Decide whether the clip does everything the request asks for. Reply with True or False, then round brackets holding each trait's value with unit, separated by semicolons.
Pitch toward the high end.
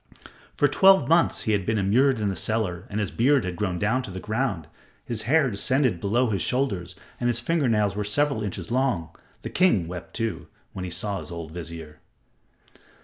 False (105 Hz)